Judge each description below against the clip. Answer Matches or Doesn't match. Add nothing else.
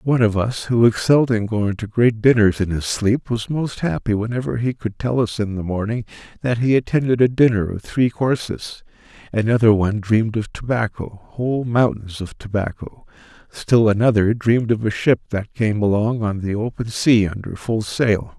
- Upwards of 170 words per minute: Matches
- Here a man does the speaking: Matches